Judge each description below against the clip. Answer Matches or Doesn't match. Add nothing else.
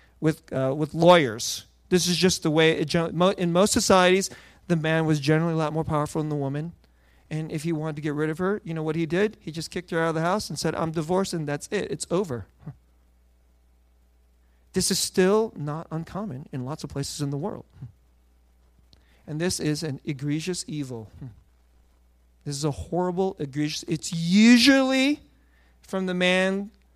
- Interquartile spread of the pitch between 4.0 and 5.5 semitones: Matches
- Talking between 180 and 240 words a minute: Matches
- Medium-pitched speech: Matches